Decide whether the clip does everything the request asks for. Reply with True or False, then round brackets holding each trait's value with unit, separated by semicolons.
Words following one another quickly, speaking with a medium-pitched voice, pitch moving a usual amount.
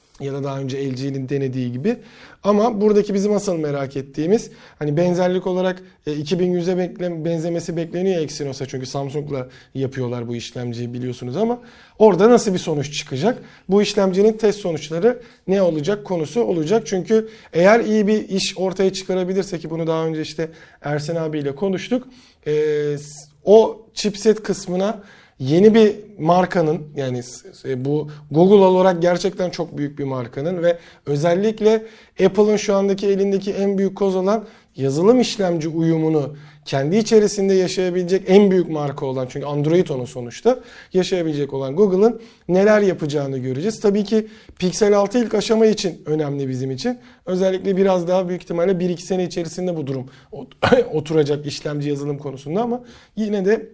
False (145 wpm; 180 Hz; 5.7 semitones)